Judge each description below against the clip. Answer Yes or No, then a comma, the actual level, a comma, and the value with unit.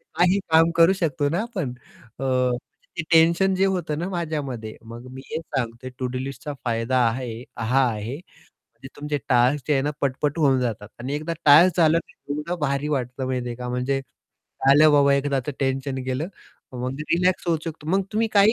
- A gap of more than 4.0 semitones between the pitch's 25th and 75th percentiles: Yes, average, 4.4 semitones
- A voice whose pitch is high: No, medium, 140 Hz